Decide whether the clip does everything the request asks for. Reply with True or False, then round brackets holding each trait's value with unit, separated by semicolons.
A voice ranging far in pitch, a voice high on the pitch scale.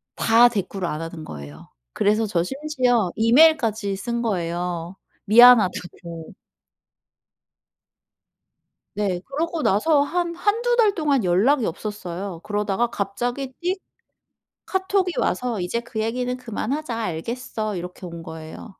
True (6.8 semitones; 225 Hz)